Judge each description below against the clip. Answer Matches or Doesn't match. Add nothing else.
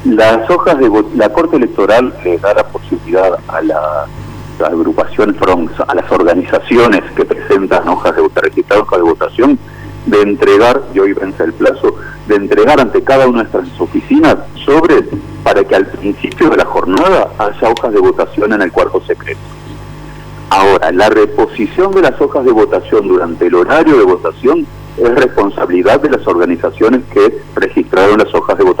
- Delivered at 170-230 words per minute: Matches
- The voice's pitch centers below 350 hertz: Doesn't match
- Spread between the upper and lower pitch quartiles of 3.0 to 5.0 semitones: Doesn't match